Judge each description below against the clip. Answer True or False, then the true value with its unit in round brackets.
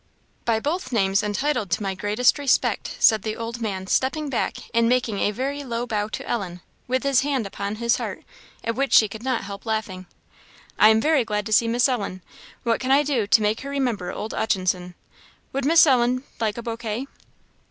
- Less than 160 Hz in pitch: False (230 Hz)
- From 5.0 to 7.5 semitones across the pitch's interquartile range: False (3.8 semitones)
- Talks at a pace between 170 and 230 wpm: True (200 wpm)